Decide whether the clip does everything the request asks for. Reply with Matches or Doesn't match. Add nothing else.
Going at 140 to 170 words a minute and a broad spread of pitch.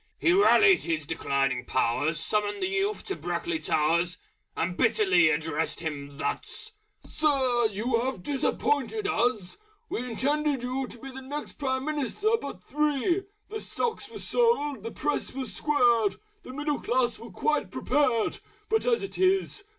Matches